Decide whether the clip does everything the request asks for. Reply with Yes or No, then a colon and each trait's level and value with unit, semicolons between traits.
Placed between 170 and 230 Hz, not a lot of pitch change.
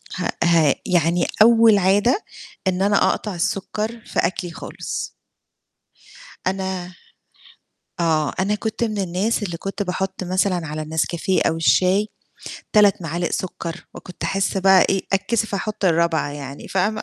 No: high, 190 Hz; average, 3.0 semitones